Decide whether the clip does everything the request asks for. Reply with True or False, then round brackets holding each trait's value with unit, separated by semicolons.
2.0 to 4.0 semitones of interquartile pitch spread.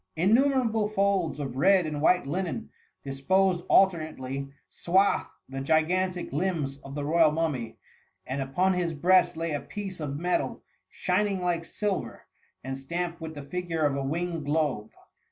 False (4.5 semitones)